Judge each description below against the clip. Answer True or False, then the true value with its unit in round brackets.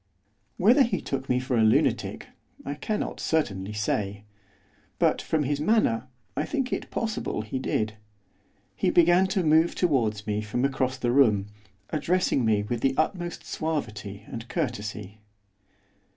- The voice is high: False (130 Hz)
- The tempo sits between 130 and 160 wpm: True (145 wpm)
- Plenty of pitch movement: True (7.1 semitones)